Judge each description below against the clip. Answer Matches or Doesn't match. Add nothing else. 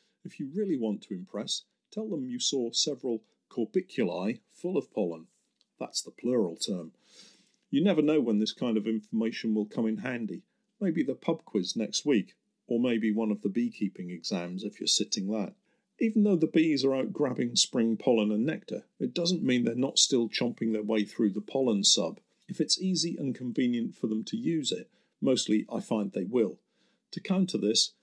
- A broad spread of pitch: Matches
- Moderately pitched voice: Doesn't match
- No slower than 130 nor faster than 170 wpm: Doesn't match